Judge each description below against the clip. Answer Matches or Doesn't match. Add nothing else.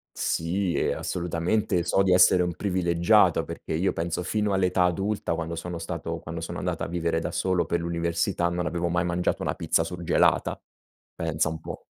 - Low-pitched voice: Matches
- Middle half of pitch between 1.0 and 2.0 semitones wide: Matches